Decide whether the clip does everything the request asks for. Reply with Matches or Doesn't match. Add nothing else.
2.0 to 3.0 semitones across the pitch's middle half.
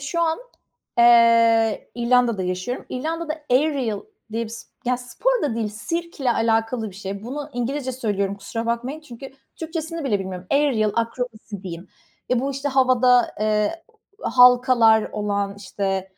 Doesn't match